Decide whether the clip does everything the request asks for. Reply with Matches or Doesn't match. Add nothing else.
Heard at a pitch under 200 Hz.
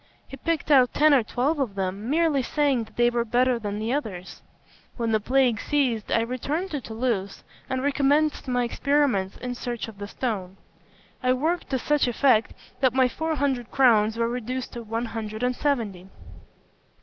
Doesn't match